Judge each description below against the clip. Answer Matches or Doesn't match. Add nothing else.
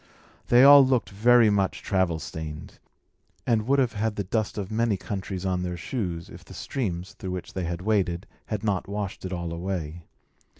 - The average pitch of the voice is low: Matches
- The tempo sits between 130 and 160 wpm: Doesn't match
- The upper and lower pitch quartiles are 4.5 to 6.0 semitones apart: Doesn't match